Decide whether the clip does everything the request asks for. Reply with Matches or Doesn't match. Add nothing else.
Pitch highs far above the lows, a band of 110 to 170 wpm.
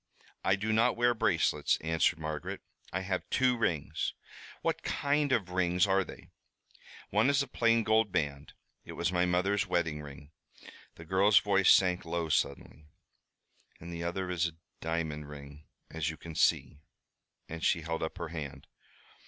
Doesn't match